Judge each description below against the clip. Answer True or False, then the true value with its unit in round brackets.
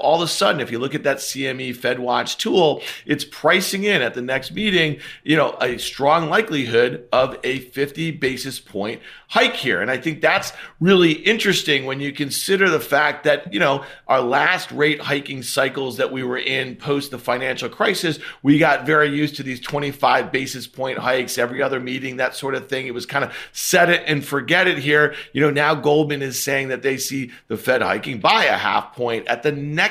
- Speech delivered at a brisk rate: True (210 wpm)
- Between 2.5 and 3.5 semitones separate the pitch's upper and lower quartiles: True (2.8 semitones)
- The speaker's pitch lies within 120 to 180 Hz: True (140 Hz)